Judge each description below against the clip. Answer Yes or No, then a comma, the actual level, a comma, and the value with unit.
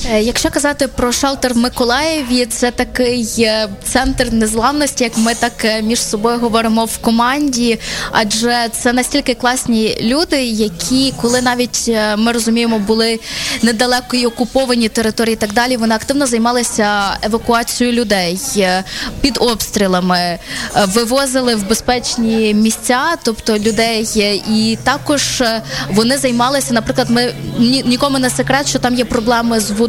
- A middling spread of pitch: No, narrow, 2.1 semitones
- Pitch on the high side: Yes, high, 235 Hz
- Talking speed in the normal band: Yes, average, 130 wpm